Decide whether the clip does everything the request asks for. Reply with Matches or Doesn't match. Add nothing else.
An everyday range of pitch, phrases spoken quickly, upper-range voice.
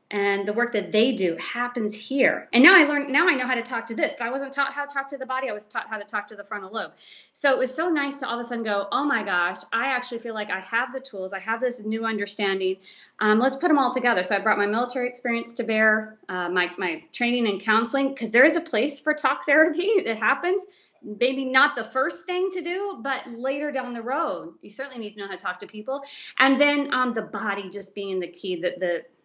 Matches